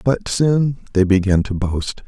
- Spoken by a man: Yes, male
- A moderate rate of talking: Yes, average, 175 wpm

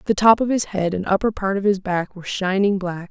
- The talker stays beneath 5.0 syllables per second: No, 5.8 syllables/s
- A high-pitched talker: Yes, high, 195 Hz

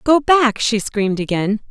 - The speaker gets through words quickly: No, average, 175 wpm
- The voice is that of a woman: Yes, female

